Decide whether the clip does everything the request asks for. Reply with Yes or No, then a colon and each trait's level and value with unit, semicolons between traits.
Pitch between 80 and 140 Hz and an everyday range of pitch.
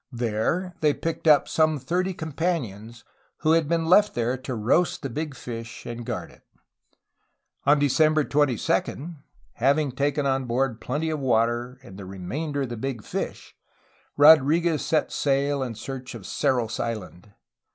Yes: low, 135 Hz; average, 4.7 semitones